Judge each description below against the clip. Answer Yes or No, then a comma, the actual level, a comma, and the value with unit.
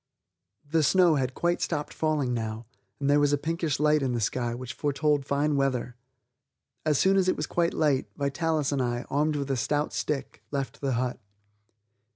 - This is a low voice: No, medium, 145 Hz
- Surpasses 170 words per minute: Yes, average, 190 wpm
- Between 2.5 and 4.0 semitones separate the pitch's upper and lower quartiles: Yes, average, 2.8 semitones